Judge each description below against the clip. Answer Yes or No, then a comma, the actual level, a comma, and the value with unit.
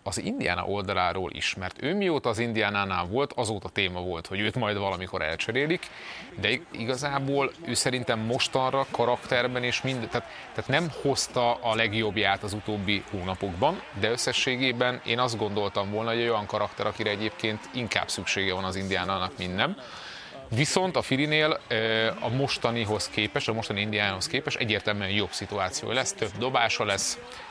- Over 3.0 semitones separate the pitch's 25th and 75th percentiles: Yes, average, 4.0 semitones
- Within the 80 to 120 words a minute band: No, fast, 155 wpm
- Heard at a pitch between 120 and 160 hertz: No, low, 110 Hz